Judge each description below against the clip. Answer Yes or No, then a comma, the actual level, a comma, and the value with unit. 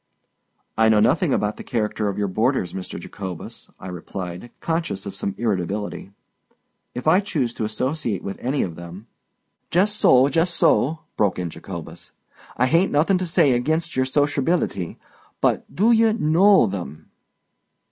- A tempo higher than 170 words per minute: No, average, 150 wpm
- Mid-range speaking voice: No, low, 120 Hz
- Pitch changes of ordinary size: No, wide, 8.7 semitones